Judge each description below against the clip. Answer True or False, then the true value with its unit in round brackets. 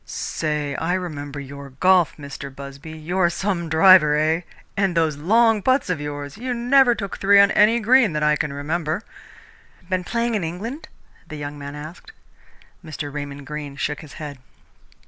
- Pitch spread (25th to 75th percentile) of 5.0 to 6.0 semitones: True (5.3 semitones)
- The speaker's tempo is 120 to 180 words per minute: True (165 wpm)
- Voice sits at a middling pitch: True (160 Hz)